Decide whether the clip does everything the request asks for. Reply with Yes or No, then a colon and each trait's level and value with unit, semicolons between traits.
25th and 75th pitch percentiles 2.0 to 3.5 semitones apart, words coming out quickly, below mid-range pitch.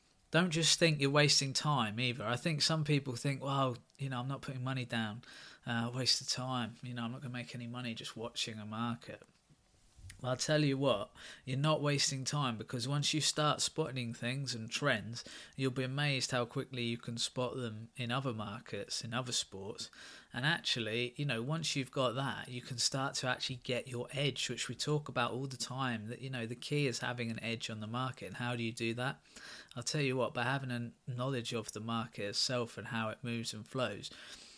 Yes: average, 2.7 semitones; fast, 220 wpm; low, 125 Hz